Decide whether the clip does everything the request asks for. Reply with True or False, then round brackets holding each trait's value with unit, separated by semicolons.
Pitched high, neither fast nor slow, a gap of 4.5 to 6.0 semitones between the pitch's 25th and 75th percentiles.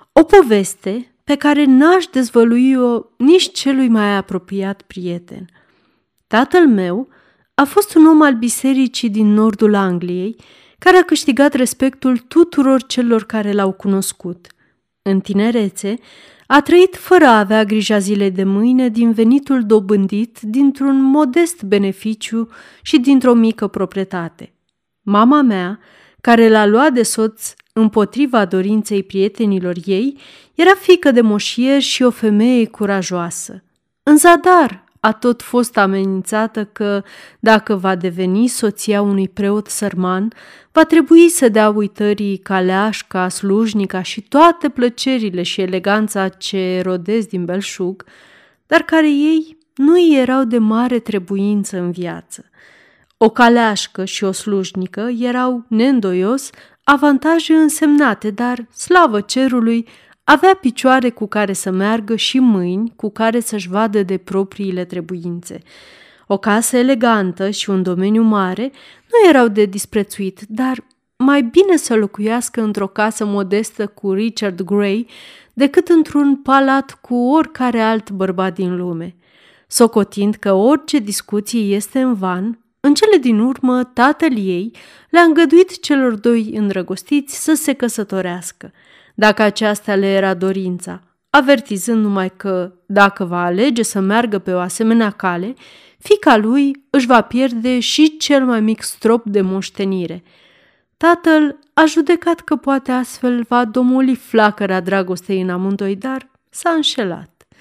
True (220 Hz; 130 wpm; 5.1 semitones)